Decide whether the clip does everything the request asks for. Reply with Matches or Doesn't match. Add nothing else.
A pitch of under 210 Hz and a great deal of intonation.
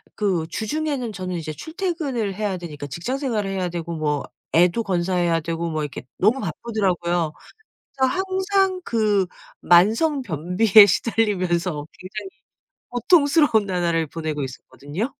Matches